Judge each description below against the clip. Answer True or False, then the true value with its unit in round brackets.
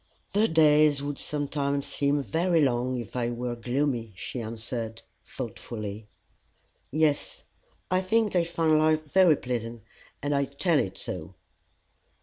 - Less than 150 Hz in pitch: True (140 Hz)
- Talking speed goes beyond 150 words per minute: False (135 wpm)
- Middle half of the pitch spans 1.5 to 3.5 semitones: False (4.8 semitones)